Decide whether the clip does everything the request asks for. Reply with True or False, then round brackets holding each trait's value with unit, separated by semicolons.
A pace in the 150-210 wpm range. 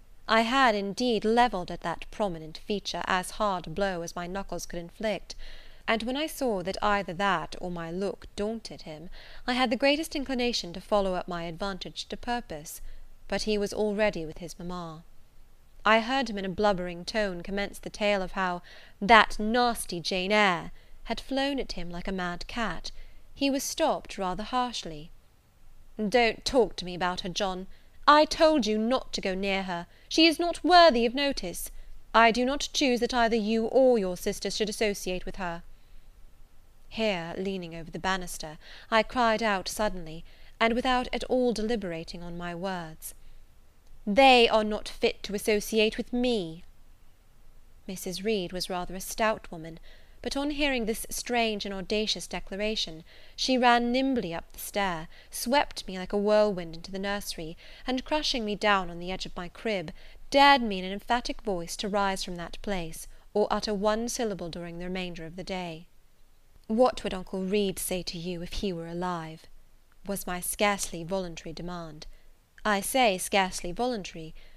True (175 wpm)